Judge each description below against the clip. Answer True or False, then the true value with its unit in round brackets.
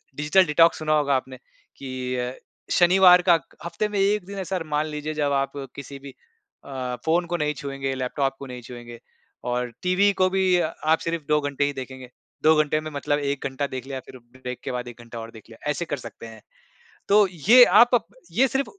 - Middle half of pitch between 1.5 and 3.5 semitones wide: False (5.0 semitones)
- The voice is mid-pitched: True (145 Hz)